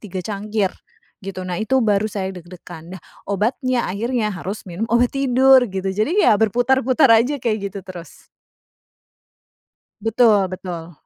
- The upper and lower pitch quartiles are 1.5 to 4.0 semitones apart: No, average, 4.4 semitones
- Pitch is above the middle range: Yes, high, 210 Hz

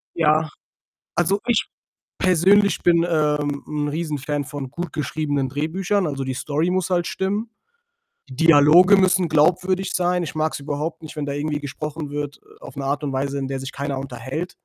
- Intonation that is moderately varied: Yes, average, 3.5 semitones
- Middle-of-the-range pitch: Yes, medium, 150 Hz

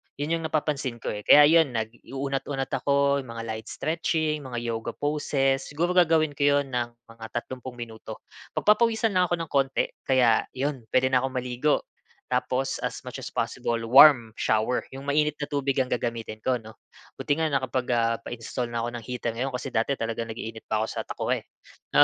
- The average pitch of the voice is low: Yes, low, 130 Hz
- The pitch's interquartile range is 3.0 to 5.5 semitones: Yes, average, 3.6 semitones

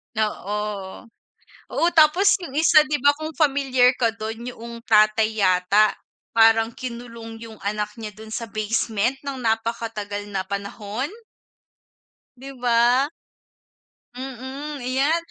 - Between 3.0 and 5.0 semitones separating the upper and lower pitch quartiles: Yes, average, 3.6 semitones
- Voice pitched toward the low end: No, high, 230 Hz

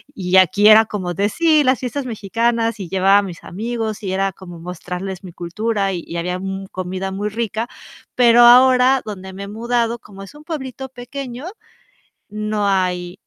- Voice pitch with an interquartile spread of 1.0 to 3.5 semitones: No, average, 4.1 semitones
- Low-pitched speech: No, high, 205 Hz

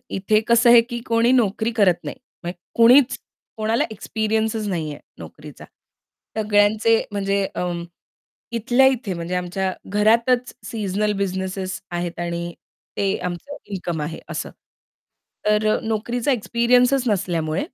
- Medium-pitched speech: No, high, 210 Hz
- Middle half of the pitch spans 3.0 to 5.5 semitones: Yes, average, 3.8 semitones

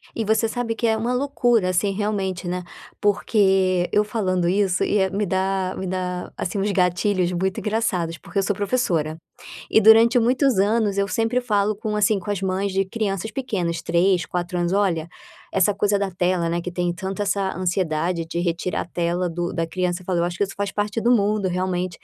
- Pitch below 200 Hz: Yes, high, 190 Hz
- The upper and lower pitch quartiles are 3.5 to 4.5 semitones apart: No, average, 2.8 semitones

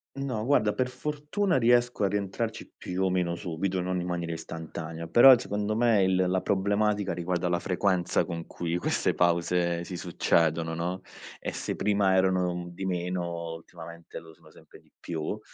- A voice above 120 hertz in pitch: No, very low, 90 Hz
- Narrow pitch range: No, average, 3.2 semitones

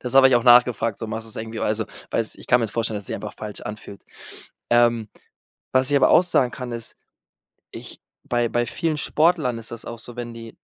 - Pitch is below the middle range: Yes, low, 120 Hz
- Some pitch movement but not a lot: No, narrow, 1.9 semitones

